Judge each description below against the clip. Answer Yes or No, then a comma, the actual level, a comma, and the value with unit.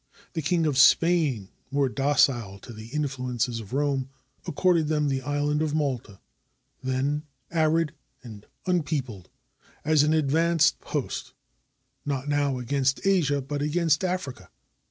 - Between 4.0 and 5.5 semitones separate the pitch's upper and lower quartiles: No, average, 3.2 semitones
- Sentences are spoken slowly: Yes, slow, 130 wpm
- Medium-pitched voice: Yes, medium, 145 Hz